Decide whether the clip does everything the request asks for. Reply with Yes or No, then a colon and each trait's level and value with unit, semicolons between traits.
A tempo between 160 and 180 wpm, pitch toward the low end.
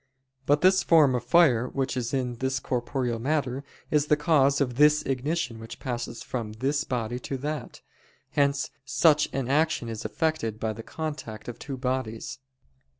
Yes: average, 165 wpm; low, 130 Hz